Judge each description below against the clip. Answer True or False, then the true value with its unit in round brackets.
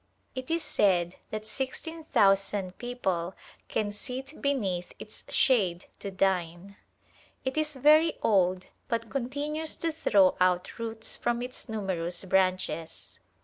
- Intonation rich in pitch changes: True (6.1 semitones)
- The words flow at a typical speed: False (125 wpm)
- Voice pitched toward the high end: True (210 Hz)